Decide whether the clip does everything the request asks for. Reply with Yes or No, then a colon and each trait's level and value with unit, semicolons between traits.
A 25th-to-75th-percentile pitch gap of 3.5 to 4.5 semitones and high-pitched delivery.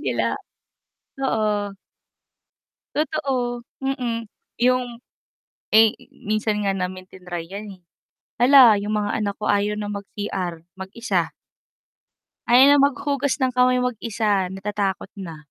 Yes: average, 4.1 semitones; high, 215 Hz